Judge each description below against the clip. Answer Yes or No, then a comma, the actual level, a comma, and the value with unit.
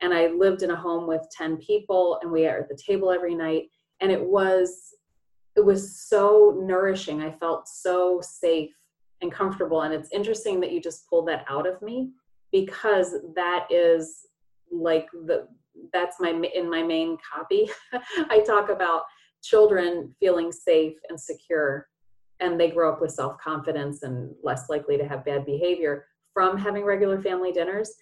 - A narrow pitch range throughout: No, average, 3.4 semitones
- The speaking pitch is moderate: Yes, medium, 175 Hz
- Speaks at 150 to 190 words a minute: Yes, average, 165 wpm